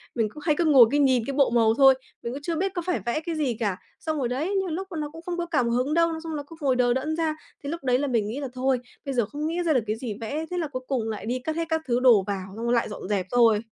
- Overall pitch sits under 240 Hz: No, very high, 270 Hz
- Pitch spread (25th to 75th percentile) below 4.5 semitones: No, average, 5.1 semitones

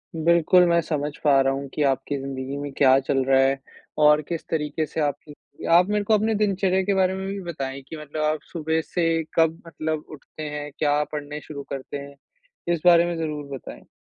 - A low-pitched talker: No, medium, 155 Hz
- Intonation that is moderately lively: Yes, average, 3.1 semitones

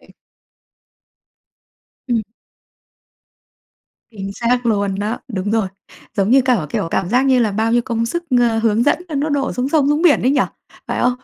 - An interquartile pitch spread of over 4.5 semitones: No, average, 3.7 semitones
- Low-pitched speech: No, high, 235 Hz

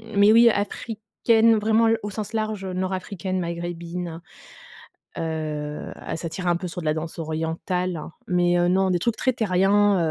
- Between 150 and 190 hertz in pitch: Yes, medium, 185 Hz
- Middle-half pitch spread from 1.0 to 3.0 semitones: No, average, 3.5 semitones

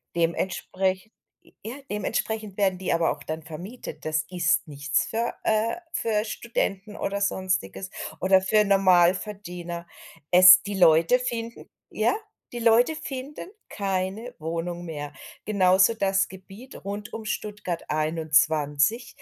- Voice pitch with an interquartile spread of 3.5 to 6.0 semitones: Yes, average, 4.0 semitones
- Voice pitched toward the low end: No, high, 190 Hz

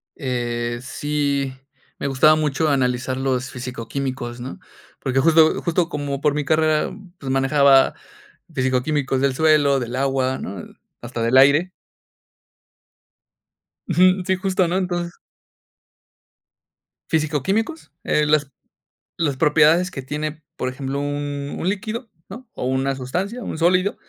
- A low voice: No, medium, 145 Hz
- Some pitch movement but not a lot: Yes, average, 3.6 semitones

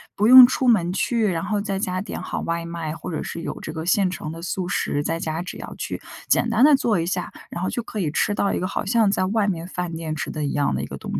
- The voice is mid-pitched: Yes, medium, 180 Hz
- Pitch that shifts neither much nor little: Yes, average, 3.8 semitones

